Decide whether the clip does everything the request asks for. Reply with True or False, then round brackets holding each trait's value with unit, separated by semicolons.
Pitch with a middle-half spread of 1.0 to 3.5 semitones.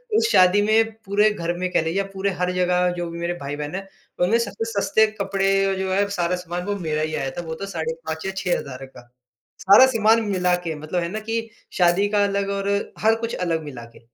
True (3.2 semitones)